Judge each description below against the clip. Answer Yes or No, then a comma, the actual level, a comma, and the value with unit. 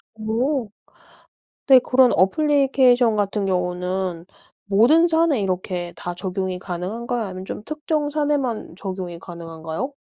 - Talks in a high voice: Yes, high, 210 Hz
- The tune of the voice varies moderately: No, wide, 6.6 semitones